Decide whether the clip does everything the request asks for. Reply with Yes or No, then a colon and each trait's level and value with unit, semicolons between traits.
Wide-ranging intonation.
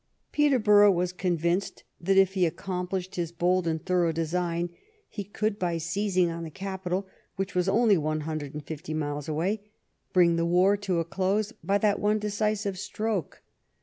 No: average, 3.1 semitones